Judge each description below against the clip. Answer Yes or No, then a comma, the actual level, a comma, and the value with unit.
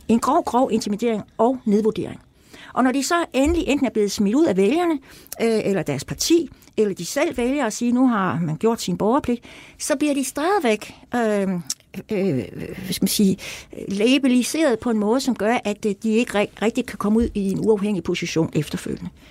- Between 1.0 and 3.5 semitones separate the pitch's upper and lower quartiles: No, average, 4.4 semitones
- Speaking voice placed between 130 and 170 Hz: No, high, 225 Hz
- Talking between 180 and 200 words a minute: Yes, average, 185 wpm